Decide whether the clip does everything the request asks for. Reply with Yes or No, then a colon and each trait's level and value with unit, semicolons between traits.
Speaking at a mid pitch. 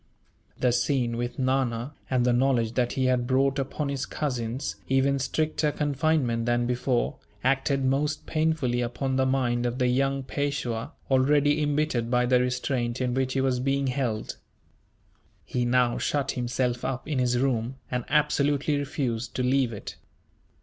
No: low, 130 Hz